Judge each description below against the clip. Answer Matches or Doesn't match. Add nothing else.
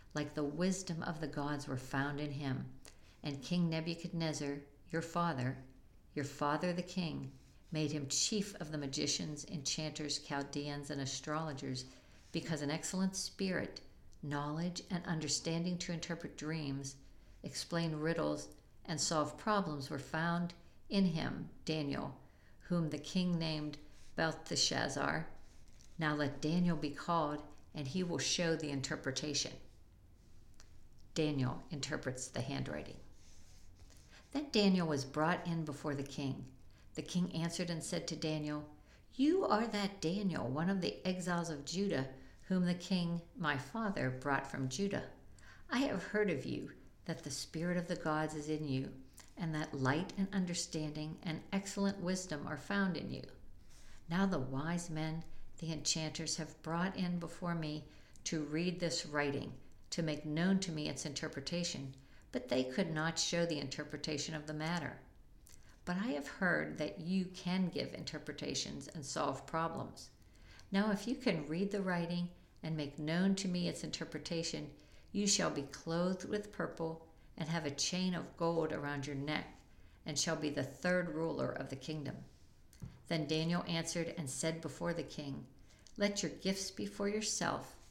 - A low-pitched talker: Doesn't match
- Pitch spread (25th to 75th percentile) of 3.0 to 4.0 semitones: Matches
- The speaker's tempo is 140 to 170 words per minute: Matches